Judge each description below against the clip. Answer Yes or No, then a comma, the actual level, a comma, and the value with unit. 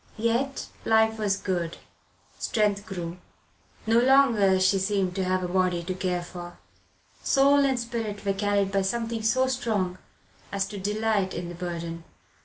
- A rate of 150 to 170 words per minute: Yes, average, 155 wpm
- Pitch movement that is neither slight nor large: Yes, average, 3.5 semitones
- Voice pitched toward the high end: Yes, high, 200 Hz